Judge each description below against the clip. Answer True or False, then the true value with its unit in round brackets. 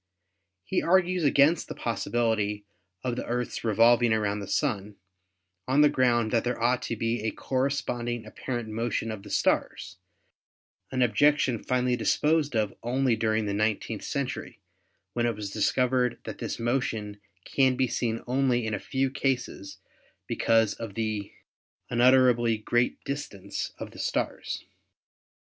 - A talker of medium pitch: False (120 Hz)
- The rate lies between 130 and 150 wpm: True (145 wpm)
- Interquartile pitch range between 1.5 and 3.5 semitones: True (2.9 semitones)